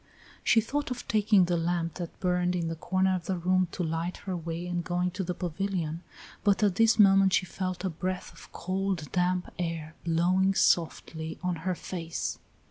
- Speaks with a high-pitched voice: No, medium, 180 Hz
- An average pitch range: No, narrow, 2.1 semitones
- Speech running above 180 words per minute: Yes, average, 190 wpm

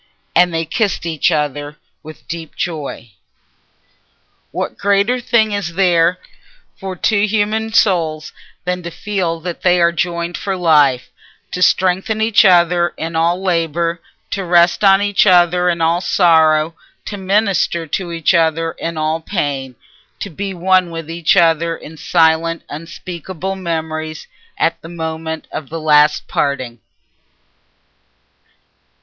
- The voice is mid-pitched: Yes, medium, 170 Hz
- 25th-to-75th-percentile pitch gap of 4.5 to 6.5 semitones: No, average, 2.7 semitones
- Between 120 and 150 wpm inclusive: Yes, slow, 135 wpm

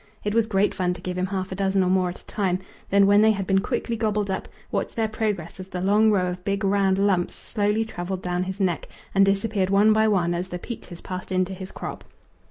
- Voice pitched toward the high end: Yes, high, 195 Hz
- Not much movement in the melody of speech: Yes, narrow, 2.1 semitones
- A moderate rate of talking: No, fast, 245 wpm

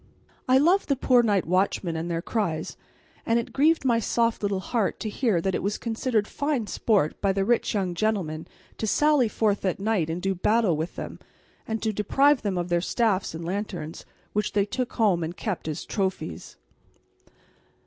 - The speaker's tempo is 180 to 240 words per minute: Yes, average, 190 wpm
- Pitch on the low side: No, high, 205 Hz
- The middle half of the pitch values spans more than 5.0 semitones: No, average, 4.6 semitones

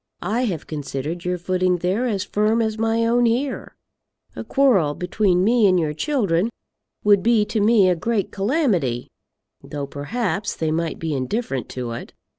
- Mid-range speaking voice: No, high, 195 Hz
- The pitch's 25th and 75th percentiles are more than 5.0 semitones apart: Yes, wide, 5.6 semitones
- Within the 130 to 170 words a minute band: Yes, average, 165 wpm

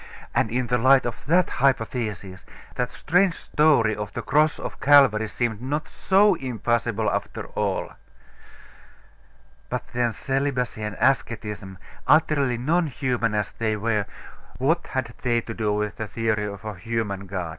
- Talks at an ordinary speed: Yes, average, 150 wpm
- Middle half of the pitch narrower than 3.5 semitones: No, average, 4.2 semitones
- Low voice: Yes, low, 120 Hz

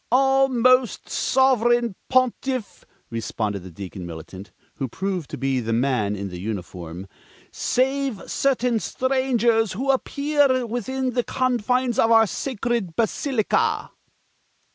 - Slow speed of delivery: Yes, slow, 120 wpm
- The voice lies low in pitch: No, high, 235 Hz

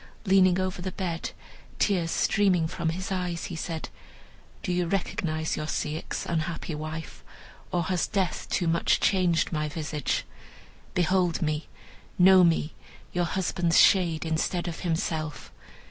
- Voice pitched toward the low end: No, medium, 170 Hz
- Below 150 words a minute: Yes, slow, 135 wpm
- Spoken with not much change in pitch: Yes, narrow, 2.3 semitones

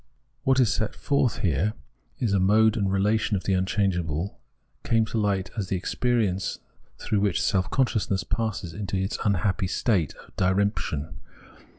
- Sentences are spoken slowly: No, average, 160 wpm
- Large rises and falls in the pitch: No, average, 2.7 semitones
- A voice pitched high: No, low, 100 Hz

